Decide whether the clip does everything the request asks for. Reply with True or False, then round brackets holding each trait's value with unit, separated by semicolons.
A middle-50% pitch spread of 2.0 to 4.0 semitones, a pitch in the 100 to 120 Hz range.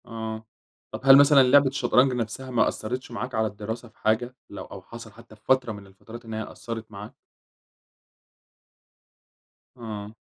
True (2.6 semitones; 115 Hz)